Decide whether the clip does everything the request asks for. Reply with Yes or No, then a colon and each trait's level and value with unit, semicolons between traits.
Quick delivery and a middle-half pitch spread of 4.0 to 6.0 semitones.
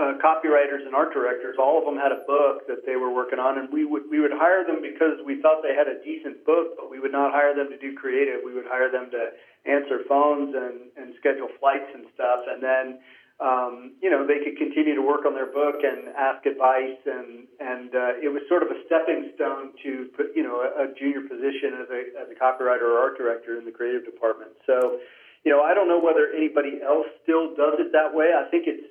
No: fast, 240 wpm; average, 3.1 semitones